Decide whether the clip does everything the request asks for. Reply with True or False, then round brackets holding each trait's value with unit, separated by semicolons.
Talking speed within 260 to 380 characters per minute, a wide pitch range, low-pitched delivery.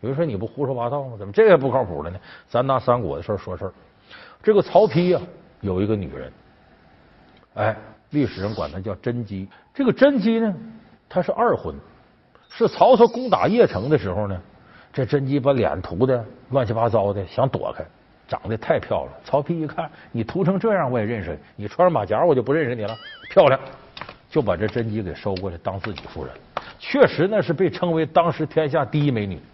True (295 characters per minute; 8.4 semitones; 125 Hz)